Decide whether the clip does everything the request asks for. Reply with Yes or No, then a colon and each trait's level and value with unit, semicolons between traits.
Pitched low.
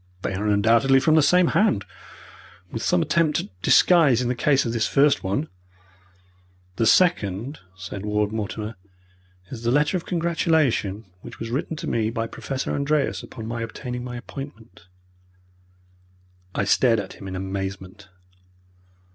Yes: low, 115 Hz